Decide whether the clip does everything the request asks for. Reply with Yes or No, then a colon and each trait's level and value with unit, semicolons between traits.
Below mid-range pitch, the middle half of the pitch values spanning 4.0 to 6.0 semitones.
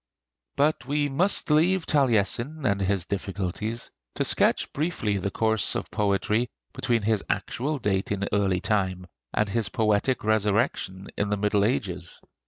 Yes: low, 105 Hz; average, 4.8 semitones